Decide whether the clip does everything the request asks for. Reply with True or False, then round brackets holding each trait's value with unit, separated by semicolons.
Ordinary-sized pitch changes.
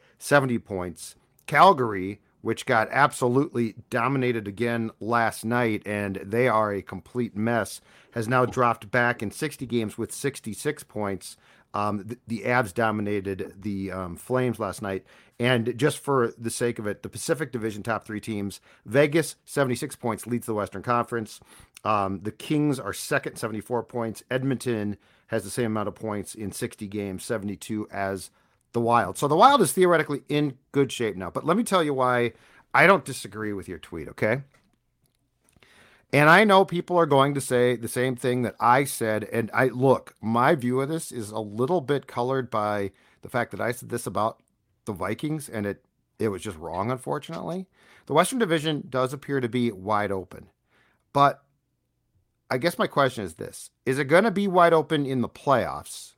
True (4.3 semitones)